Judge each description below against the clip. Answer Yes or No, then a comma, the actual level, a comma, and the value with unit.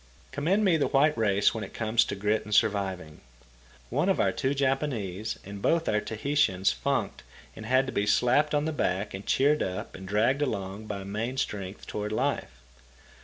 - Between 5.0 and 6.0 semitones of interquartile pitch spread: Yes, wide, 5.5 semitones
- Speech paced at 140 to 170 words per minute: No, average, 185 wpm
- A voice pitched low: Yes, low, 110 Hz